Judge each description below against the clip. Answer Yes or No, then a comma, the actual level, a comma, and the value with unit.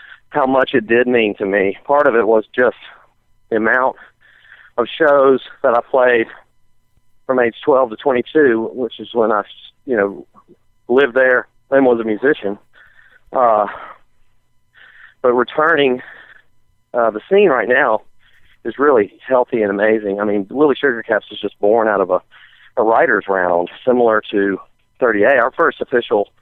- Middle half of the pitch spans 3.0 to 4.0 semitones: Yes, average, 3.6 semitones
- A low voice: Yes, low, 115 Hz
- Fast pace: No, average, 155 wpm